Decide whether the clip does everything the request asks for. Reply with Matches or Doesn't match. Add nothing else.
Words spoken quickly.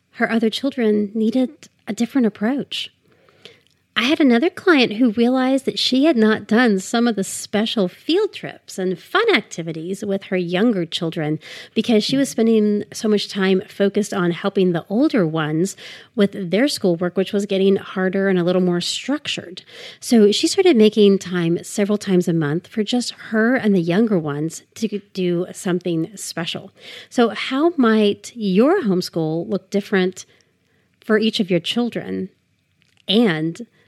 Doesn't match